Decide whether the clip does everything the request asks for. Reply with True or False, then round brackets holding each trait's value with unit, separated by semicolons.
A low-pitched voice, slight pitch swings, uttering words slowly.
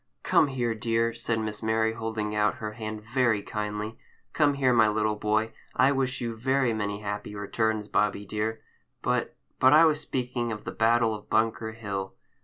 False (110 Hz; 2.0 semitones; 175 wpm)